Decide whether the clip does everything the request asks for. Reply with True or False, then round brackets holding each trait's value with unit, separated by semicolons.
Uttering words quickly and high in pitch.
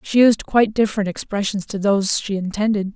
False (185 wpm; 205 Hz)